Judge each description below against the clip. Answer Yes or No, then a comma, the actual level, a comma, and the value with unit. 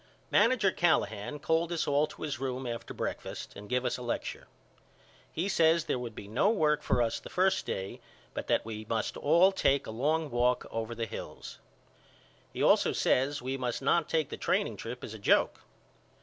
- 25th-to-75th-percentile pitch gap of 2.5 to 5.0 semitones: No, wide, 5.4 semitones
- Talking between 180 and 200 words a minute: Yes, average, 190 wpm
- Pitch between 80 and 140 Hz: Yes, low, 135 Hz